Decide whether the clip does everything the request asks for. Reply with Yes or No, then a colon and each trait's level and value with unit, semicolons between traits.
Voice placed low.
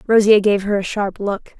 No: high, 205 Hz